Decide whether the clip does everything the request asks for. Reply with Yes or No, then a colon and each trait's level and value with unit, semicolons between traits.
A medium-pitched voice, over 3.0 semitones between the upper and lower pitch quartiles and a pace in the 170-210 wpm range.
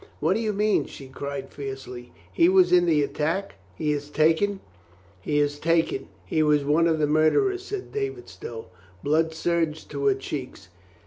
Yes: medium, 155 Hz; average, 3.9 semitones; average, 175 wpm